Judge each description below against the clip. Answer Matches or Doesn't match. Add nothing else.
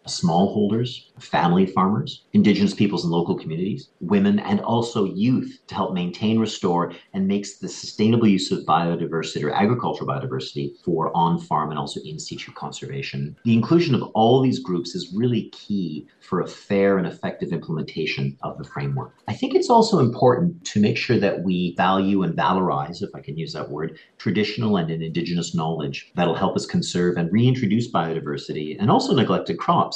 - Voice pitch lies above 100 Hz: Doesn't match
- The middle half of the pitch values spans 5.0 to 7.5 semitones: Matches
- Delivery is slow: Doesn't match